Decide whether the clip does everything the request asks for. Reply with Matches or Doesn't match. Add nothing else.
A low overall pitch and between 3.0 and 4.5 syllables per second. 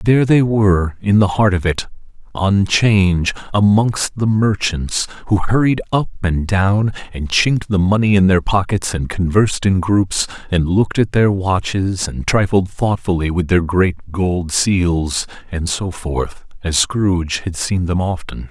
Matches